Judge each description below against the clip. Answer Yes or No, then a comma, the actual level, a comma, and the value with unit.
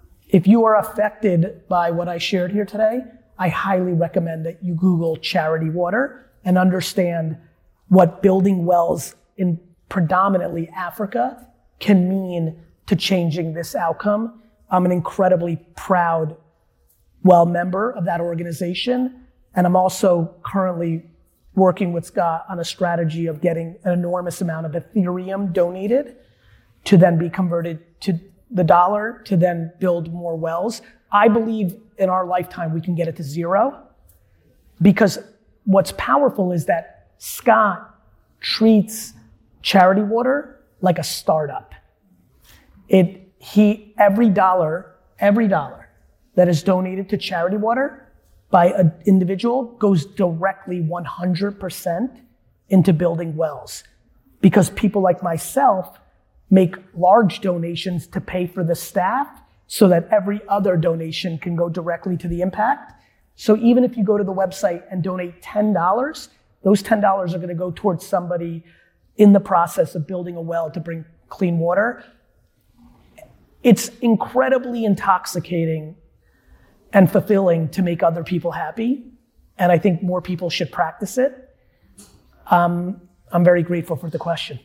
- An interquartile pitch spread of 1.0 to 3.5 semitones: Yes, average, 3.0 semitones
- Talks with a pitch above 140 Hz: Yes, medium, 185 Hz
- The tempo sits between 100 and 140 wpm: Yes, slow, 135 wpm